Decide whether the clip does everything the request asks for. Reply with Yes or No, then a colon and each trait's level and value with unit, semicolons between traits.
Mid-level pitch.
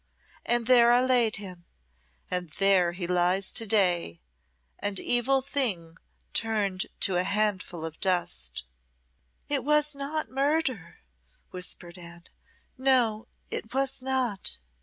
No: high, 210 Hz